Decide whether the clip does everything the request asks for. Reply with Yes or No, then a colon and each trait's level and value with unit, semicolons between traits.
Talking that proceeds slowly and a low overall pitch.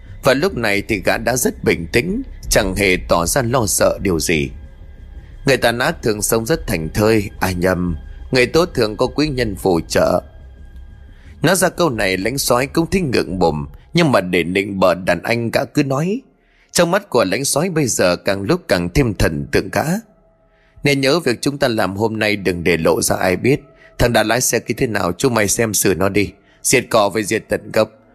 No: average, 215 wpm; low, 110 Hz